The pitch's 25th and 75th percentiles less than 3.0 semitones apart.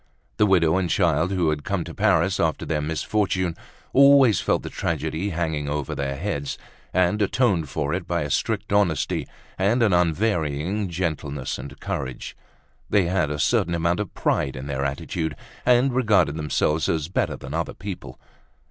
No: average, 5.0 semitones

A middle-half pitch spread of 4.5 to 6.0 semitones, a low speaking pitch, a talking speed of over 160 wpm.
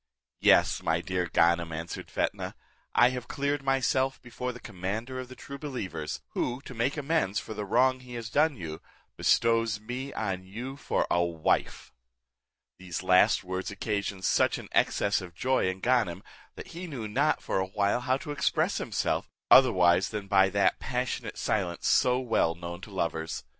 Yes: wide, 5.6 semitones; low, 110 Hz; average, 175 wpm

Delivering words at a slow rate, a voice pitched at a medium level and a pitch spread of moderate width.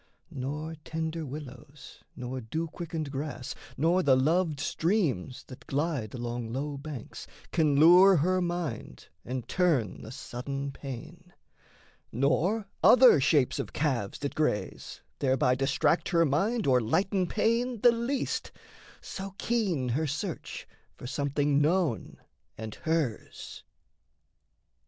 Yes: slow, 120 wpm; medium, 150 Hz; average, 4.9 semitones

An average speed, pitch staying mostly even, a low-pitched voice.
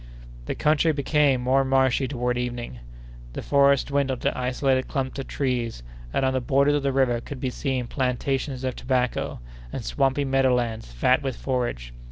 Yes: average, 175 wpm; narrow, 1.8 semitones; low, 130 Hz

